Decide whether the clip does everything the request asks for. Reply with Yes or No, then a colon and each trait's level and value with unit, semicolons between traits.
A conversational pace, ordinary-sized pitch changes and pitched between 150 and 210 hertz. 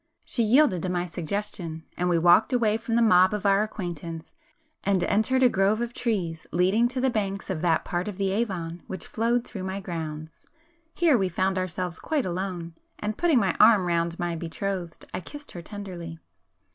Yes: average, 195 wpm; average, 4.0 semitones; high, 190 Hz